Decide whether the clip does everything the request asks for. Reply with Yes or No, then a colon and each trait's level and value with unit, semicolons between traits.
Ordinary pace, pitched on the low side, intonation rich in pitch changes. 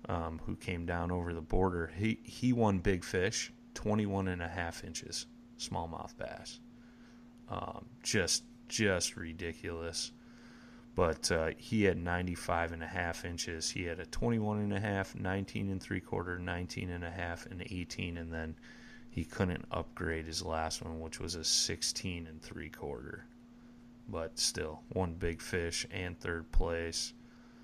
Yes: average, 150 wpm; very low, 90 Hz; wide, 5.7 semitones